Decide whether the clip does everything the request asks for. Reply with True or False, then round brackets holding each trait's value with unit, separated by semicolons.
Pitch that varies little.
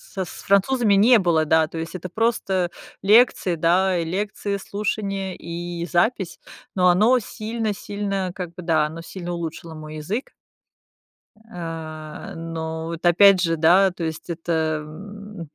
False (3.4 semitones)